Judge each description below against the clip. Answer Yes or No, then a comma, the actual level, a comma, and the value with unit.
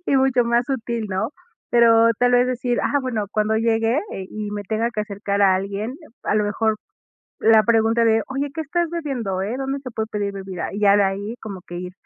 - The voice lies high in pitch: Yes, high, 225 Hz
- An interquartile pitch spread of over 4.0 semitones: No, average, 3.3 semitones